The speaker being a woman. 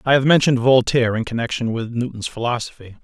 No: male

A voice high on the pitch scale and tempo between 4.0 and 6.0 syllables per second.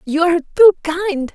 Yes: very high, 335 Hz; 4.9 syllables/s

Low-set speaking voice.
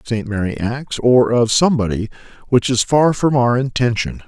Yes: low, 120 Hz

